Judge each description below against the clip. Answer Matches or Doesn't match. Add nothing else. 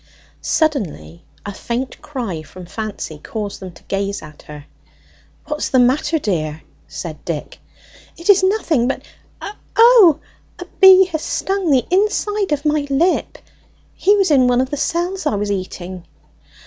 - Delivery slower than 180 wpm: Matches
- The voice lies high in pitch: Matches